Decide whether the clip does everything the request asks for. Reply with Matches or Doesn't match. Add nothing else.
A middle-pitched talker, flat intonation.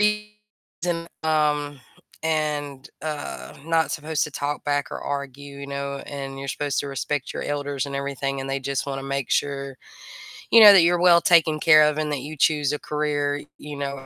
Matches